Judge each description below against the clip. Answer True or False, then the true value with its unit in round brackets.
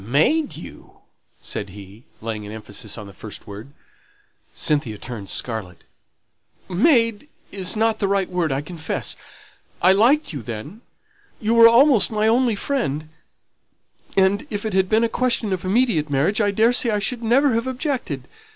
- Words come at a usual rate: True (160 wpm)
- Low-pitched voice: False (200 Hz)